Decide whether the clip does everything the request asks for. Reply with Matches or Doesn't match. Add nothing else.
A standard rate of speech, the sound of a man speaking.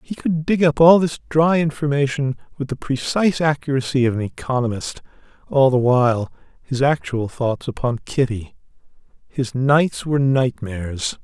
Matches